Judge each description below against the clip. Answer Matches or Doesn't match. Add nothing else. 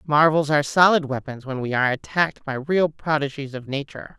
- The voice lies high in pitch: Doesn't match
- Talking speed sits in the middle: Matches